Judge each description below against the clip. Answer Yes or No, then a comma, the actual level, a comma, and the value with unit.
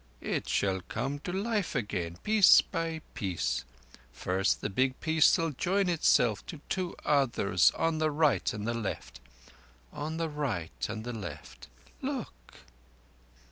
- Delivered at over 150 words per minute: No, average, 140 wpm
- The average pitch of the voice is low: Yes, low, 125 Hz